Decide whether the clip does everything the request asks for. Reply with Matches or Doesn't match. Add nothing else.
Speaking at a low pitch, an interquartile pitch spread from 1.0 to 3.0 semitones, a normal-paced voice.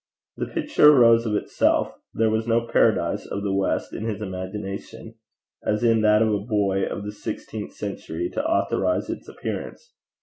Matches